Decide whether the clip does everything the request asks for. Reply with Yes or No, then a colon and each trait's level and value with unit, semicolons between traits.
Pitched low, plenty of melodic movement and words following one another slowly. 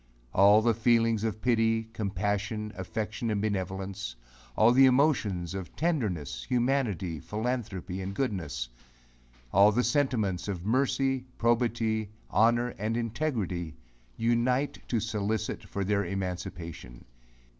No: low, 110 Hz; average, 3.6 semitones; slow, 115 wpm